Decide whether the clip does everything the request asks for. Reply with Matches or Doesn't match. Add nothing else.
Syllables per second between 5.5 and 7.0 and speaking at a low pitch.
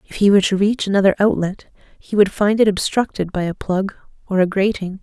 Doesn't match